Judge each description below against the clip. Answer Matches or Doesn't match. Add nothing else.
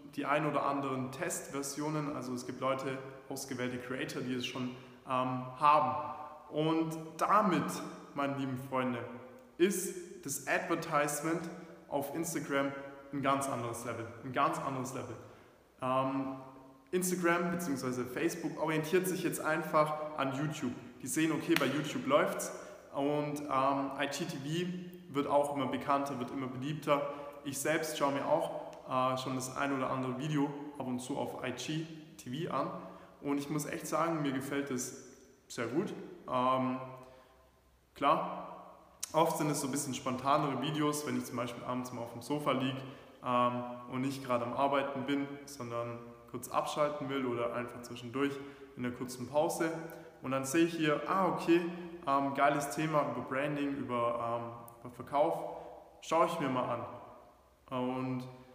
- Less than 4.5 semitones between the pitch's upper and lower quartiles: Matches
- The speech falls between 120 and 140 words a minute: Doesn't match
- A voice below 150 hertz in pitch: Matches